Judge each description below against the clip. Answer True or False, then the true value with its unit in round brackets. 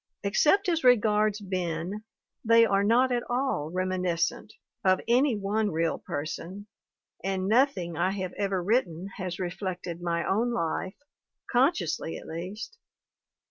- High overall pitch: True (195 Hz)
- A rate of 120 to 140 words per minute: True (135 wpm)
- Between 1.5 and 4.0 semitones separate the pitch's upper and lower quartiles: False (4.6 semitones)